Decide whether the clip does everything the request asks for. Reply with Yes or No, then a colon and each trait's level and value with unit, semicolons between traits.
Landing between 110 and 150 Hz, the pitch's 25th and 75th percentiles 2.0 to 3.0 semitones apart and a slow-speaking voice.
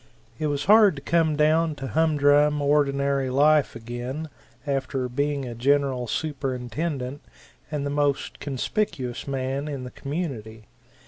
Yes: medium, 140 Hz; narrow, 2.5 semitones; slow, 130 wpm